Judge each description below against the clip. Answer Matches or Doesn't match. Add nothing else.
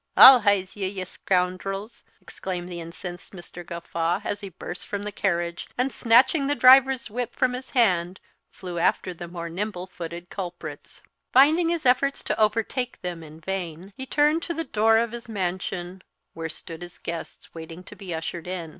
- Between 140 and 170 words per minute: Doesn't match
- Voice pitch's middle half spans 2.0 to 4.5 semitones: Doesn't match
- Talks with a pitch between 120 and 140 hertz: Doesn't match